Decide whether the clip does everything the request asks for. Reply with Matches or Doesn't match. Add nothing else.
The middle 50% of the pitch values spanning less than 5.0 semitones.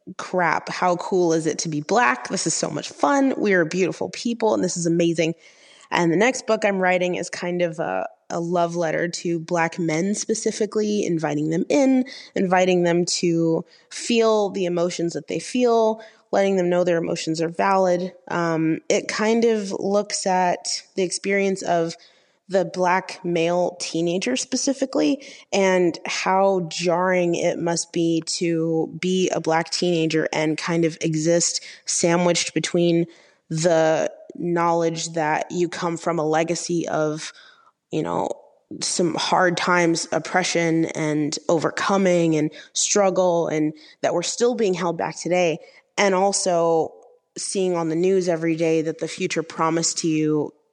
Matches